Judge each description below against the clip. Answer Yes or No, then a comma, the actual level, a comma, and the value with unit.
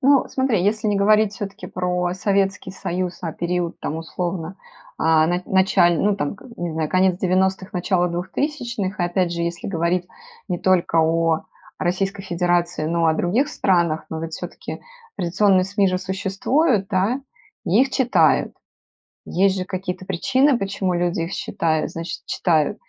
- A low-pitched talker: No, medium, 185 Hz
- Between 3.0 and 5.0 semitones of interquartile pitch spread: No, narrow, 2.4 semitones